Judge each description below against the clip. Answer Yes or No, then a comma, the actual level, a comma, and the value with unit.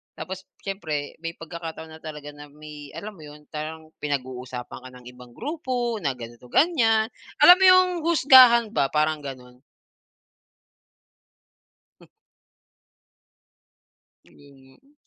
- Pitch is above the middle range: No, medium, 155 Hz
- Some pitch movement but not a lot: No, wide, 8.1 semitones